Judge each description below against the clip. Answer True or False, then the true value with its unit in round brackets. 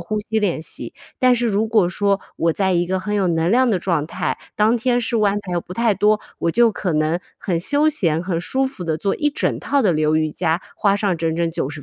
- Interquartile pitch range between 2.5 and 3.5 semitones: False (4.7 semitones)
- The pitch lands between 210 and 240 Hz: False (190 Hz)